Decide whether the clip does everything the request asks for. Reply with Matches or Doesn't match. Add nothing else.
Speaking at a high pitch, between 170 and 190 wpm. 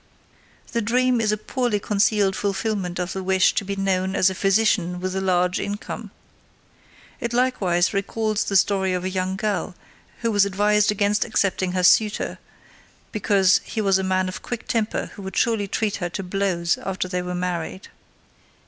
Matches